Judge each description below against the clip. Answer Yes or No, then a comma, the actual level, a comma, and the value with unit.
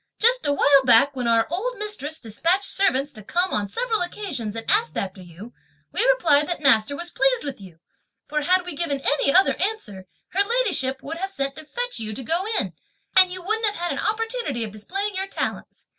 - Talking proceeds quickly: Yes, fast, 210 wpm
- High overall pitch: Yes, very high, 330 Hz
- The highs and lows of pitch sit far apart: Yes, wide, 7.7 semitones